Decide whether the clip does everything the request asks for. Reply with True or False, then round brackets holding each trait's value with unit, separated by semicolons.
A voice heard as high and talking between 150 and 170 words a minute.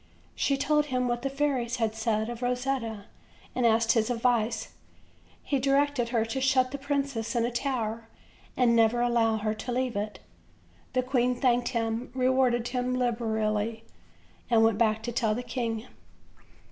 True (240 Hz; 165 wpm)